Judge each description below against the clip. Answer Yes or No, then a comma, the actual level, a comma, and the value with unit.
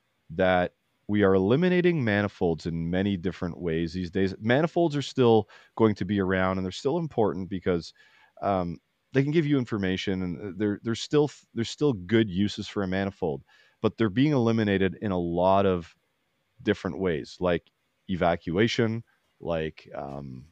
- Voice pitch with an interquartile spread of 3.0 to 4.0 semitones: Yes, average, 3.7 semitones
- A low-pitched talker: Yes, low, 100 Hz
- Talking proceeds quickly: No, average, 160 wpm